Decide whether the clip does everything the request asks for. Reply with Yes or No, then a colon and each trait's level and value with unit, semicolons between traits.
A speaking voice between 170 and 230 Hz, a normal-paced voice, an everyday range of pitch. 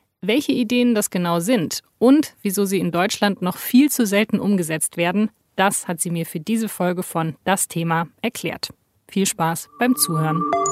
Yes: high, 190 Hz; average, 175 wpm; average, 5.0 semitones